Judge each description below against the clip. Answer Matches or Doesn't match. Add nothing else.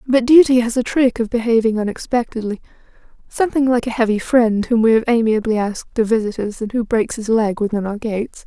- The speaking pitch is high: Matches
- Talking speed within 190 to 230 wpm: Matches